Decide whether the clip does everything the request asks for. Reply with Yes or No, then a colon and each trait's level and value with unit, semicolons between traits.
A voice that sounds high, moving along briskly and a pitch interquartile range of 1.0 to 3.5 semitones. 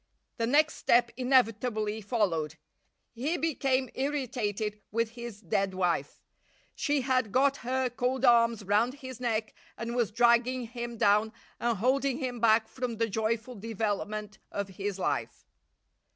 No: high, 235 Hz; slow, 135 wpm; average, 3.1 semitones